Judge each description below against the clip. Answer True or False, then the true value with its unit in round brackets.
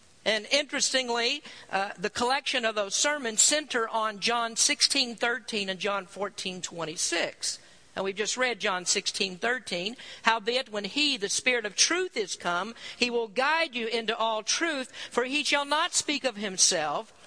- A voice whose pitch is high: True (235 Hz)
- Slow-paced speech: False (155 wpm)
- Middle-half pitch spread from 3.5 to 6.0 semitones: True (4.5 semitones)